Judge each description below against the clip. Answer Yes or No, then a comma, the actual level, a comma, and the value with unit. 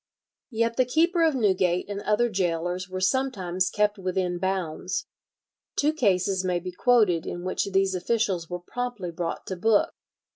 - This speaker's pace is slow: No, average, 155 wpm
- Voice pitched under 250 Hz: Yes, high, 190 Hz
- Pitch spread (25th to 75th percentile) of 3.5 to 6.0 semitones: Yes, average, 4.2 semitones